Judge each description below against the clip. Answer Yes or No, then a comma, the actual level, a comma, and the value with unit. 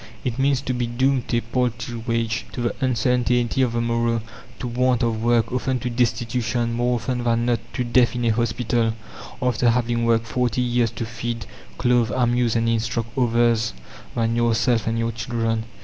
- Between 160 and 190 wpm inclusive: Yes, average, 180 wpm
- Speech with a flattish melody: Yes, narrow, 1.2 semitones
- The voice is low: Yes, low, 120 Hz